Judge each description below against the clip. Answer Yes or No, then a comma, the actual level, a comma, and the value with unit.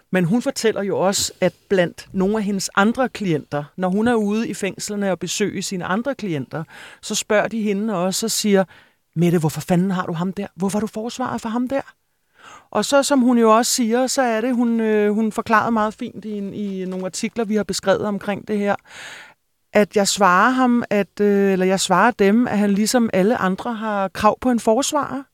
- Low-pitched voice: No, high, 210 Hz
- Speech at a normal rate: Yes, average, 210 wpm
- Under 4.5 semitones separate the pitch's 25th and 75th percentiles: Yes, average, 3.4 semitones